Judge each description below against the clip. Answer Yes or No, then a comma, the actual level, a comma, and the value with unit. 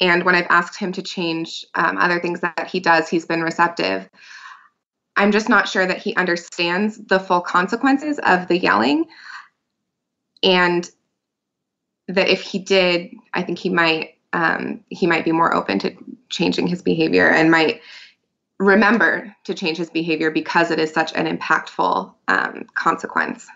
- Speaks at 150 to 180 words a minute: Yes, average, 160 wpm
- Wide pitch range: No, average, 2.7 semitones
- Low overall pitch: No, medium, 175 Hz